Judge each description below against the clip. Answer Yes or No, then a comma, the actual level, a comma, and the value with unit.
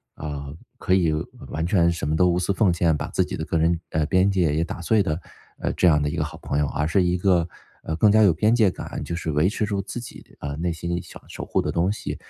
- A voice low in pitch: Yes, very low, 85 Hz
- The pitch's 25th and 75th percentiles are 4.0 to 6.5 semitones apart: No, average, 3.2 semitones